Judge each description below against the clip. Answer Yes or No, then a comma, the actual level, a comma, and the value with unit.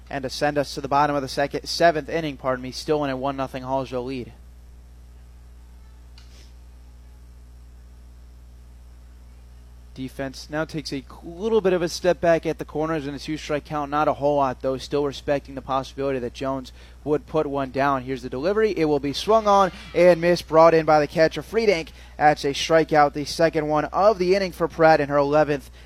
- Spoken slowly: No, average, 190 wpm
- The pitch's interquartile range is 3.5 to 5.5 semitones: Yes, average, 4.4 semitones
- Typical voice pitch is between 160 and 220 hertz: No, medium, 140 Hz